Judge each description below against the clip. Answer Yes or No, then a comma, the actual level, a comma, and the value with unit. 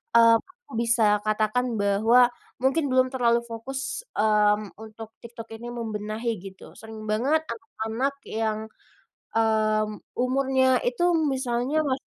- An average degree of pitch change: Yes, average, 3.1 semitones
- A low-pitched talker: No, high, 230 Hz